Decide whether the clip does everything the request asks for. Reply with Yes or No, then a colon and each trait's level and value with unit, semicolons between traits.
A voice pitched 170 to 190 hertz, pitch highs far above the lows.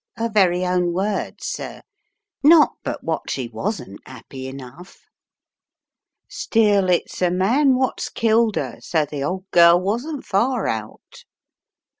Yes: medium, 185 Hz; wide, 6.0 semitones